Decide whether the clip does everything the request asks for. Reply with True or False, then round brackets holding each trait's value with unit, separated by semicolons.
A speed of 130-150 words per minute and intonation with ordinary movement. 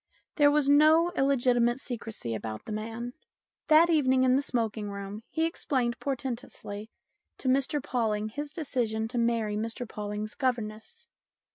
True (140 wpm; 4.4 semitones)